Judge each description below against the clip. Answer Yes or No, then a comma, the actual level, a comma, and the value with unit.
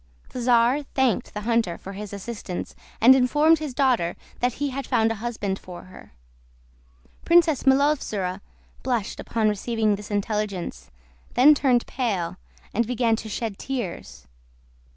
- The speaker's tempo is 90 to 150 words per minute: Yes, average, 140 wpm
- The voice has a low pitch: No, high, 230 Hz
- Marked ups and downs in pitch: No, average, 4.4 semitones